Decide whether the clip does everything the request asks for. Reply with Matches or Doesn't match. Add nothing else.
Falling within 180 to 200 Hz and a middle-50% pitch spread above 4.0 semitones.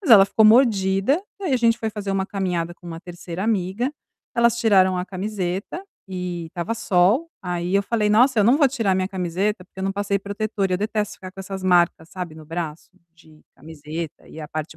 Doesn't match